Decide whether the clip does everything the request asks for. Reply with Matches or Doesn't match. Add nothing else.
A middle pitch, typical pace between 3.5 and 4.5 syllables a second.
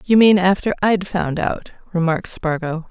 Doesn't match